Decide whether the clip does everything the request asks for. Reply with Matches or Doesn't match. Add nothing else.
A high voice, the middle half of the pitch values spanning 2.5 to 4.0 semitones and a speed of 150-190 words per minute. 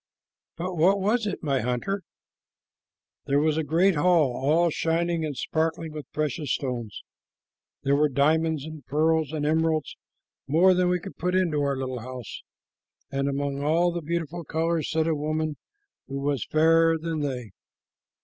Doesn't match